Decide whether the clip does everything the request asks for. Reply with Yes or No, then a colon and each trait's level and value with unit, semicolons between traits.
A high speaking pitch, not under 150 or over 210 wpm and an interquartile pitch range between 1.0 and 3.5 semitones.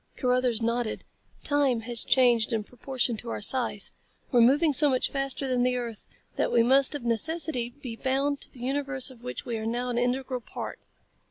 Yes: very high, 250 Hz; average, 190 wpm; narrow, 2.4 semitones